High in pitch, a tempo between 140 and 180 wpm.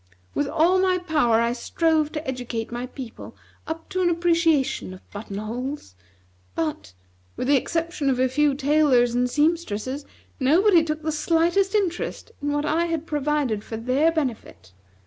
Yes: very high, 295 Hz; average, 160 wpm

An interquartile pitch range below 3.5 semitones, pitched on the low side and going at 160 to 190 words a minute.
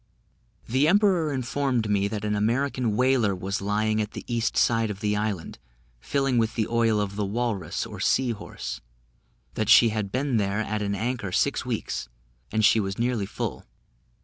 Yes: average, 3.1 semitones; low, 110 Hz; average, 175 wpm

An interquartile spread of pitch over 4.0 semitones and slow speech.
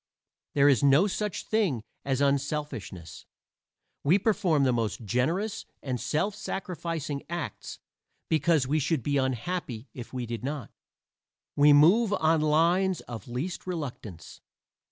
Yes: wide, 5.4 semitones; slow, 130 wpm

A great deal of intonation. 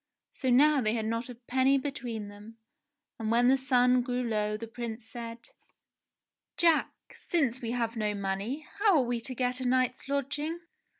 No: average, 2.7 semitones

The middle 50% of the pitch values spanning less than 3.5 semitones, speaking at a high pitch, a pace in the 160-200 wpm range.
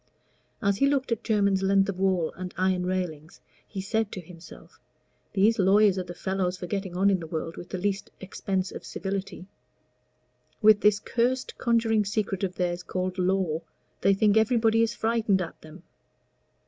Yes: narrow, 2.6 semitones; high, 195 Hz; average, 175 wpm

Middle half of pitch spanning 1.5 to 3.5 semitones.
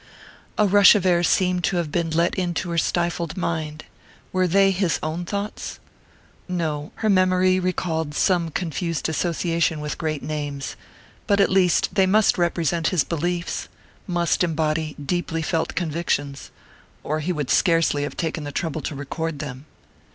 Yes: average, 2.8 semitones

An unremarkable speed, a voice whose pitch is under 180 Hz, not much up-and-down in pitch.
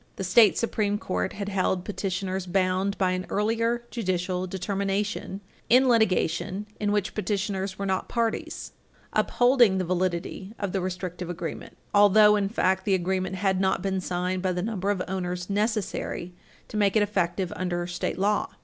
No: average, 160 wpm; high, 190 Hz; narrow, 2.1 semitones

